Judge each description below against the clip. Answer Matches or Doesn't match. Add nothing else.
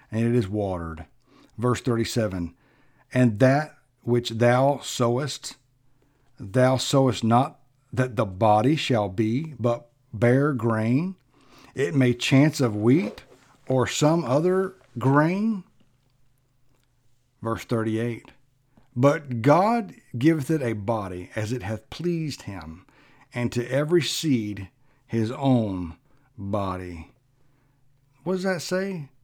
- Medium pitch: Doesn't match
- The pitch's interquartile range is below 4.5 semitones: Matches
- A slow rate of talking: Matches